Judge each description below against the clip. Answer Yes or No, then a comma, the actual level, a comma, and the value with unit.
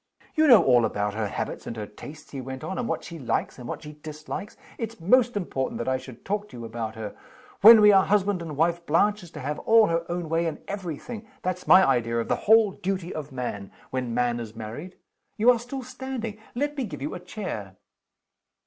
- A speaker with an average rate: No, fast, 230 wpm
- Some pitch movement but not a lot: No, wide, 8.8 semitones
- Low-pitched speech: No, medium, 165 Hz